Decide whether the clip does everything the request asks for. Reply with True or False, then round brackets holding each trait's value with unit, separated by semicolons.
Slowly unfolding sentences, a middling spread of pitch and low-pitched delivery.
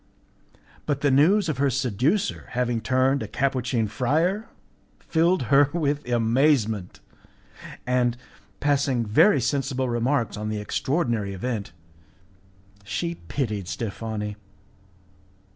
True (105 wpm; 4.3 semitones; 130 Hz)